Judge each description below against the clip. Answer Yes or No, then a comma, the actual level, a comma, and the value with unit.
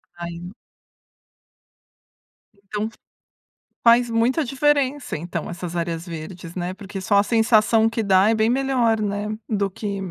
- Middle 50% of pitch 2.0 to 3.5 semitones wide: No, average, 4.2 semitones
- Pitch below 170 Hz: No, high, 205 Hz